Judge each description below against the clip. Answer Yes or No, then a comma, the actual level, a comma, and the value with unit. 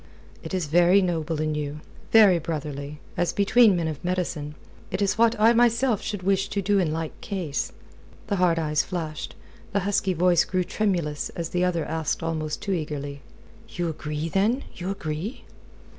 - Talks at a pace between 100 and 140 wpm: No, average, 175 wpm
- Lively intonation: No, average, 4.2 semitones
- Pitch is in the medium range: Yes, medium, 175 Hz